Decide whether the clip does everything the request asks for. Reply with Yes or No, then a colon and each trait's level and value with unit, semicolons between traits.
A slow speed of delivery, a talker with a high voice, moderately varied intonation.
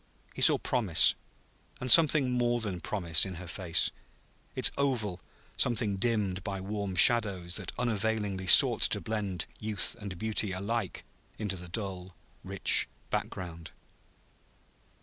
No: slow, 130 wpm; low, 100 Hz; average, 3.4 semitones